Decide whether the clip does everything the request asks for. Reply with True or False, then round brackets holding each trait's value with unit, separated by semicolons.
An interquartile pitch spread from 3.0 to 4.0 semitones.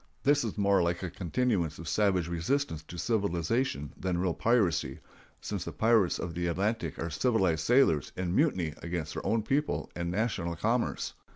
False (5.1 semitones)